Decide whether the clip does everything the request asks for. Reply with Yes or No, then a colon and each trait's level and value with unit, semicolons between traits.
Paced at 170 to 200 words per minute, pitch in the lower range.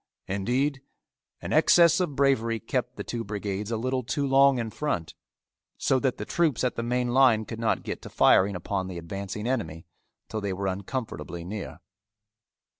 Yes: average, 175 wpm; low, 115 Hz